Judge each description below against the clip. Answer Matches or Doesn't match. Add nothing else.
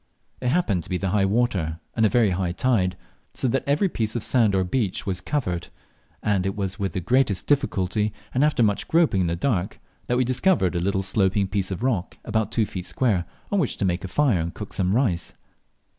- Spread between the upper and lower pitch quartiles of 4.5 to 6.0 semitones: Matches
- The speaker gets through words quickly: Matches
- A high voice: Doesn't match